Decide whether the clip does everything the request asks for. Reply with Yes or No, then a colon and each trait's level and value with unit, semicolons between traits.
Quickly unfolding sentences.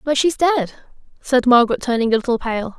No: average, 195 wpm